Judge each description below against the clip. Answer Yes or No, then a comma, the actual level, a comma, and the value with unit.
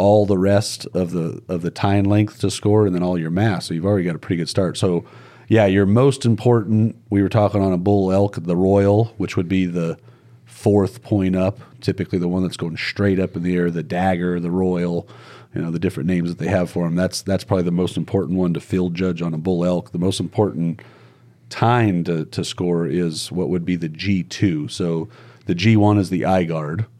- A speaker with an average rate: No, fast, 230 wpm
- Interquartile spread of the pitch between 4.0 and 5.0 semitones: No, average, 2.8 semitones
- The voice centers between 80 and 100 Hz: Yes, very low, 95 Hz